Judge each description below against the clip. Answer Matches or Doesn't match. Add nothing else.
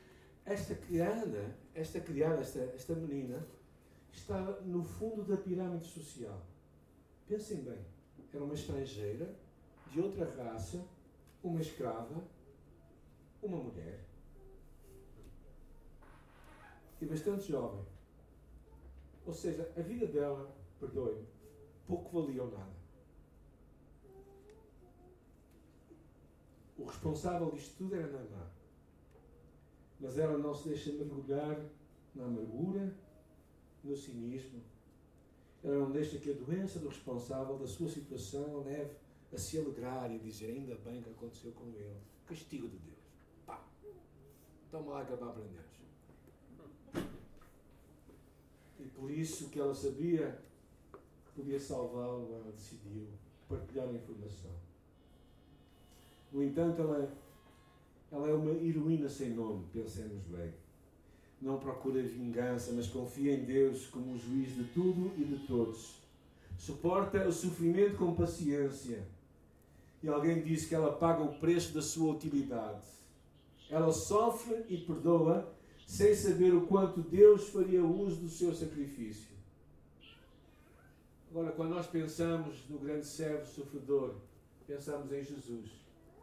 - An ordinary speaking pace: Doesn't match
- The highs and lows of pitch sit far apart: Matches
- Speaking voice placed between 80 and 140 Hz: Matches